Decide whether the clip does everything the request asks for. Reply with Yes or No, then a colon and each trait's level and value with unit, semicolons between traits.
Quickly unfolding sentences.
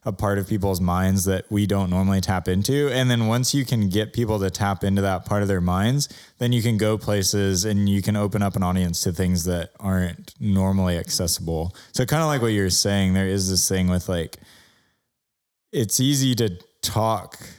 Yes: fast, 210 wpm